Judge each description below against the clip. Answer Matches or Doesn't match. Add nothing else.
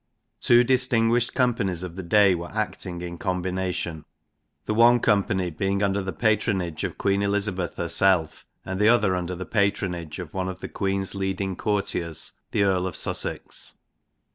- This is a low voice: Matches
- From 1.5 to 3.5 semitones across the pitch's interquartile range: Matches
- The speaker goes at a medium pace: Matches